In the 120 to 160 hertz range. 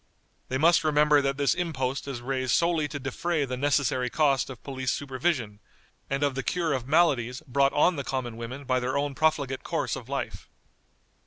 Yes: low, 135 Hz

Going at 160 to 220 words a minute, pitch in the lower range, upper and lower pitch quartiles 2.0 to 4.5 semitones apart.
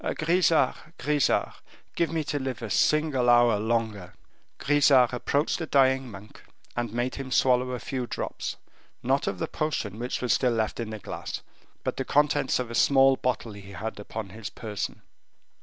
Yes: average, 175 wpm; low, 125 Hz; average, 4.0 semitones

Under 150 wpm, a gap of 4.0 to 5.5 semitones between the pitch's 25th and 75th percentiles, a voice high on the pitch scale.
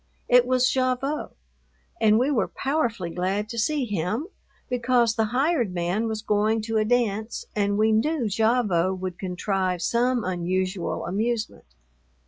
Yes: average, 140 wpm; average, 4.6 semitones; high, 220 Hz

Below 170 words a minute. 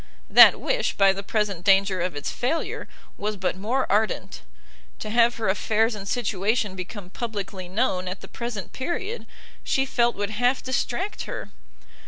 Yes: average, 160 wpm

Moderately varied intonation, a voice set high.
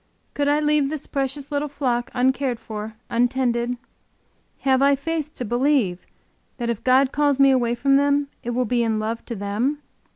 Yes: average, 3.1 semitones; very high, 260 Hz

